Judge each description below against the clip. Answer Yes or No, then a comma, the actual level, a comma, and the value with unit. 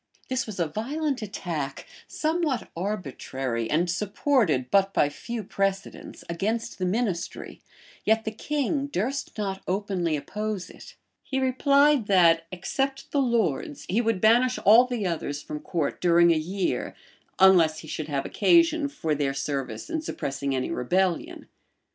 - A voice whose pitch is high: Yes, high, 195 Hz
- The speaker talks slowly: No, average, 150 wpm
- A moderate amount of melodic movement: No, wide, 7.1 semitones